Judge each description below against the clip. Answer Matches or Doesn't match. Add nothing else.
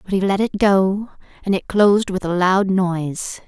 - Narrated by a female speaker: Matches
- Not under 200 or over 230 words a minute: Matches